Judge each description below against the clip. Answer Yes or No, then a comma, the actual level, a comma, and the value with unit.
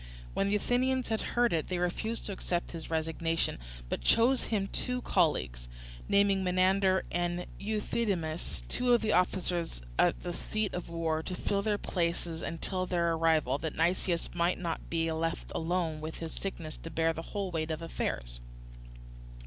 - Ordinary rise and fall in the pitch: Yes, average, 3.4 semitones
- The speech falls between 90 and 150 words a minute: No, average, 165 wpm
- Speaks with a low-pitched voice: No, medium, 175 Hz